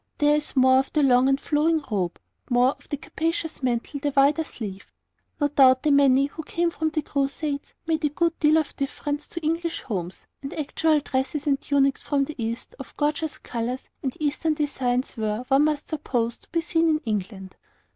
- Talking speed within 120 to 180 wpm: No, average, 195 wpm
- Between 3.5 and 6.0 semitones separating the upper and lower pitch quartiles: No, average, 3.1 semitones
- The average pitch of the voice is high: Yes, very high, 285 Hz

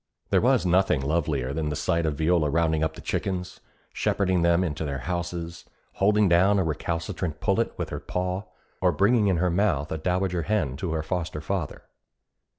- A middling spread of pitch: Yes, average, 3.0 semitones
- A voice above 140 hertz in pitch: No, very low, 85 Hz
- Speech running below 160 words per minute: No, average, 180 wpm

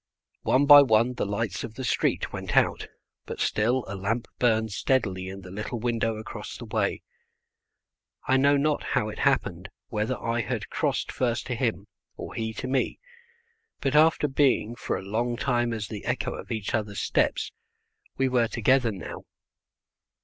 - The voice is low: Yes, low, 115 Hz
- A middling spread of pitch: Yes, average, 3.2 semitones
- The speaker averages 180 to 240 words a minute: No, average, 170 wpm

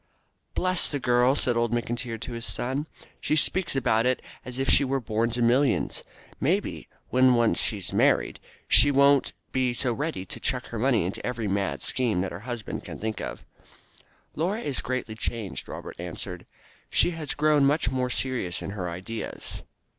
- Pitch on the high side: No, low, 125 Hz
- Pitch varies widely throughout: No, average, 3.6 semitones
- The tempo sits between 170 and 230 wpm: Yes, average, 180 wpm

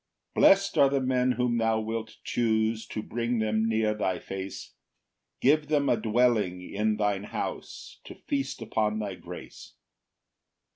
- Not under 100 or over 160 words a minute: Yes, average, 150 wpm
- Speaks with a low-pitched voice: Yes, low, 110 Hz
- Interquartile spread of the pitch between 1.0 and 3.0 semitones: Yes, narrow, 2.6 semitones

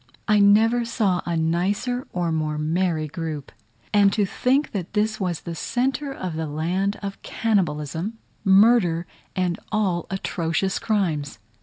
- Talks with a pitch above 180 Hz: Yes, high, 190 Hz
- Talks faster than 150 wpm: No, average, 145 wpm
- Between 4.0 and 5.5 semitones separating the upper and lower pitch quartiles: Yes, average, 4.6 semitones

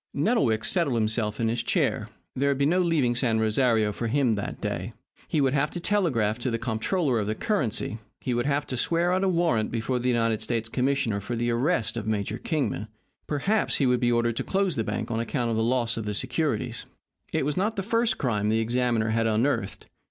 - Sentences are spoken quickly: Yes, fast, 220 wpm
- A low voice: Yes, low, 120 Hz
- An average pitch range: Yes, average, 4.4 semitones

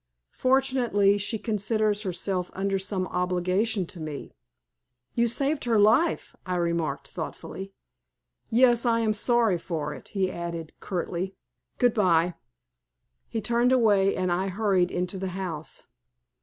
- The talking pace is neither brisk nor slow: No, slow, 130 wpm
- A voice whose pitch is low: No, high, 195 Hz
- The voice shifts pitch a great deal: No, average, 4.0 semitones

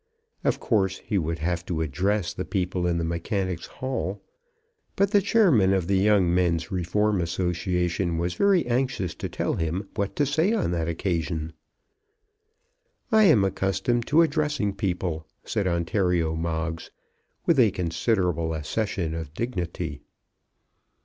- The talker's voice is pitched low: Yes, very low, 95 Hz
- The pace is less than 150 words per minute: Yes, average, 140 wpm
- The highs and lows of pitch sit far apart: No, average, 4.1 semitones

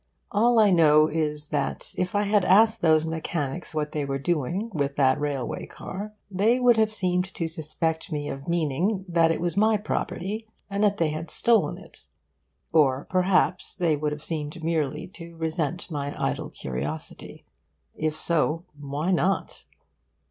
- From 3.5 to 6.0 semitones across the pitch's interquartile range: Yes, average, 4.2 semitones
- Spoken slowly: No, average, 165 wpm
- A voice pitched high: No, medium, 165 Hz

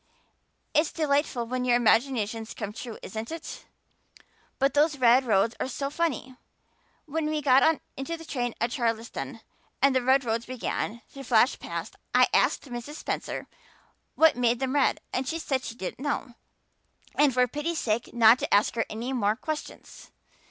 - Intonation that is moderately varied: Yes, average, 3.6 semitones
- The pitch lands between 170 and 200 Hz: No, very high, 255 Hz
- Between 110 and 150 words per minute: No, average, 165 wpm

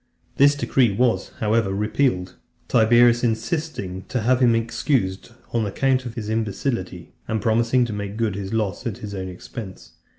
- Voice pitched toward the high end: No, low, 115 Hz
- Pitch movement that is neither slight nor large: Yes, average, 3.3 semitones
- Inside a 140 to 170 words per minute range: Yes, average, 160 wpm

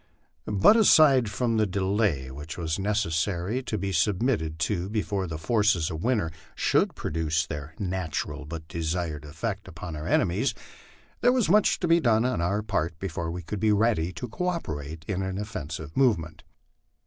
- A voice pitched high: No, very low, 95 Hz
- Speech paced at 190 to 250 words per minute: No, average, 165 wpm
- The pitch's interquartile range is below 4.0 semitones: No, average, 5.2 semitones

